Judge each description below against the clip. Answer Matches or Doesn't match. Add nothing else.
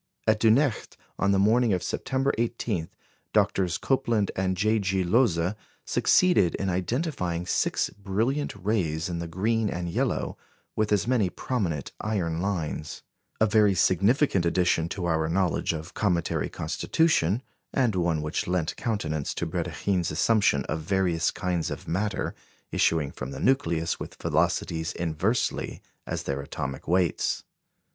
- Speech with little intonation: Doesn't match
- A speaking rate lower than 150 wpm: Matches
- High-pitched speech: Doesn't match